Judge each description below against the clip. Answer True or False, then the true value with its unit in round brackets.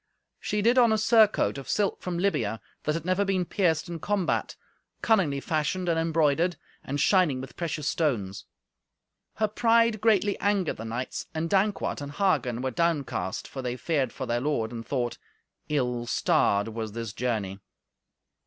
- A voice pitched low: False (155 Hz)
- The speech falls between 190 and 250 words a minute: False (160 wpm)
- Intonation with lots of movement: True (7.7 semitones)